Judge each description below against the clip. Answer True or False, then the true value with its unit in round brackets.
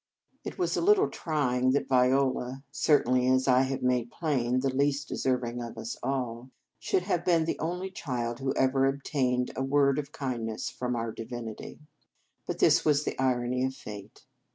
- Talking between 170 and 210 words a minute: True (175 wpm)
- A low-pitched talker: True (130 Hz)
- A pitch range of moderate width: False (2.3 semitones)